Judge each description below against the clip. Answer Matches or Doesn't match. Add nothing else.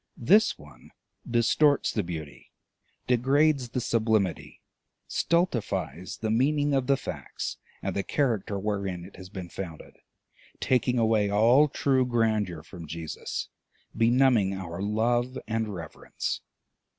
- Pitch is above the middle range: Doesn't match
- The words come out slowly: Matches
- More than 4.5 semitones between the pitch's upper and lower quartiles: Matches